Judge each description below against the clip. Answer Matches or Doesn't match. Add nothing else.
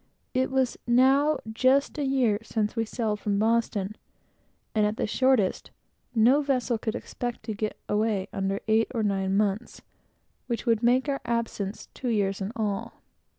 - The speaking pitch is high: Matches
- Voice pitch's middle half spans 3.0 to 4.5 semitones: Matches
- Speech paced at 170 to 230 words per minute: Doesn't match